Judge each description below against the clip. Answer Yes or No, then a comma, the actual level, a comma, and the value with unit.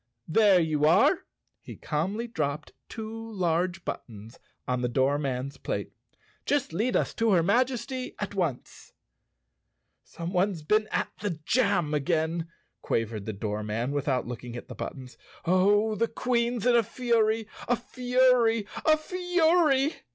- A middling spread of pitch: No, wide, 8.3 semitones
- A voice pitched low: No, high, 195 Hz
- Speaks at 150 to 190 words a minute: No, slow, 135 wpm